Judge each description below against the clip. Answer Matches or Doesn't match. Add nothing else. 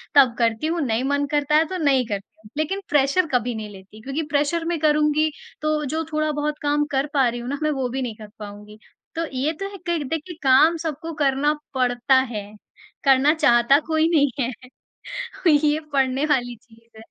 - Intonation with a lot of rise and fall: Doesn't match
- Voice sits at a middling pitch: Doesn't match